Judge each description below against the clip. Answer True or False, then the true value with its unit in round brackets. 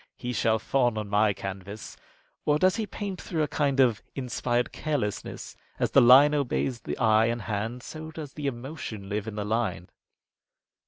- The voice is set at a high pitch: False (120 Hz)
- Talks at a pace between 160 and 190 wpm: True (180 wpm)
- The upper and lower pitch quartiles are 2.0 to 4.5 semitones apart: False (5.2 semitones)